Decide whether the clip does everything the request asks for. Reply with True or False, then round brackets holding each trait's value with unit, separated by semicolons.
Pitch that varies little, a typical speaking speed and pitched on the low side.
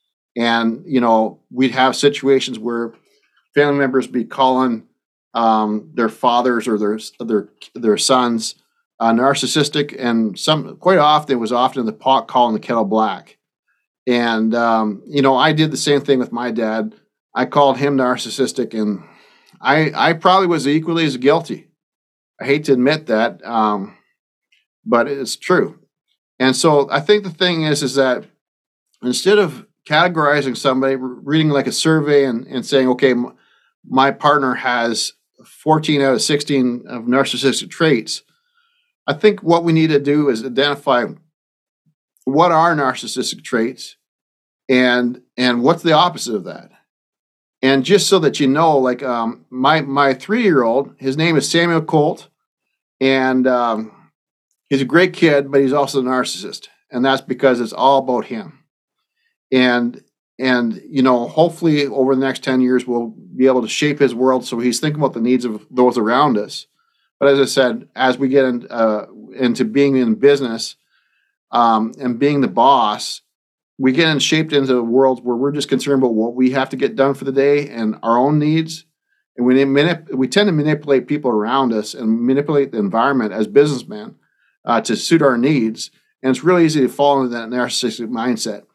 False (3.1 semitones; 170 wpm; 130 Hz)